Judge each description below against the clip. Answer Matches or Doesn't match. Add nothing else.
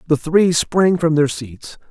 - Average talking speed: Matches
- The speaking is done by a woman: Doesn't match